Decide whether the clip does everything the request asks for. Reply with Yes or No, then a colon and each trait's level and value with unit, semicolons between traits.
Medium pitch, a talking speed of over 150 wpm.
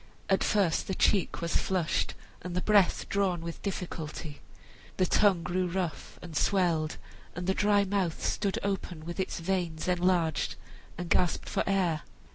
Yes: medium, 180 Hz; average, 160 wpm